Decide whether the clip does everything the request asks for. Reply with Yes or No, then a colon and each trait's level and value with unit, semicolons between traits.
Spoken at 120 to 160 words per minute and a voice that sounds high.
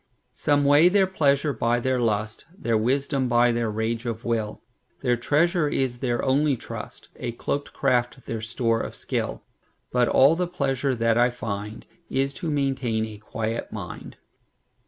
No: average, 140 wpm; low, 125 Hz